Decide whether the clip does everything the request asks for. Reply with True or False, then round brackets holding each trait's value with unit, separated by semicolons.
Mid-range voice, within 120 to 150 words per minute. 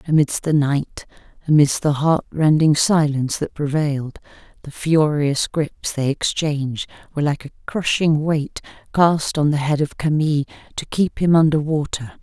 True (150 Hz; 145 wpm)